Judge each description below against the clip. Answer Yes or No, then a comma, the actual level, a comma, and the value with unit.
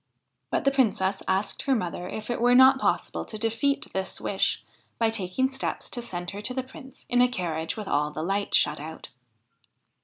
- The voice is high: Yes, high, 215 Hz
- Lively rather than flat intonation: Yes, wide, 5.7 semitones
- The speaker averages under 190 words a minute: No, average, 195 wpm